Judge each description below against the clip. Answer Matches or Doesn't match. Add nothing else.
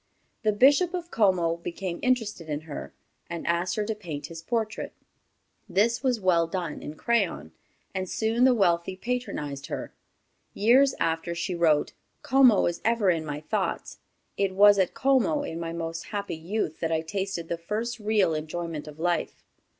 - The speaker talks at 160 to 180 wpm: Matches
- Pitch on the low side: Doesn't match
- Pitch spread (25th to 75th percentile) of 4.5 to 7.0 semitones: Matches